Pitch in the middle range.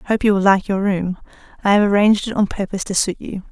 No: high, 200 Hz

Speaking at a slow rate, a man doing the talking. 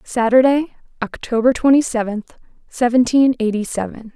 No: slow, 100 wpm; female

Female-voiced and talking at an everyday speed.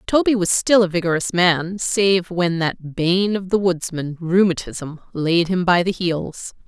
Yes: female; average, 170 wpm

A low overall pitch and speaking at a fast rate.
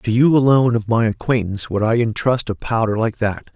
Yes: low, 115 Hz; fast, 220 wpm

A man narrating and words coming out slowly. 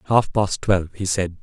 No: male; fast, 210 wpm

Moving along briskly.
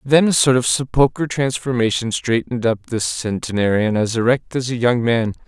No: average, 175 wpm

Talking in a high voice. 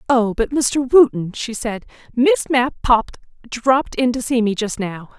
Yes: high, 245 Hz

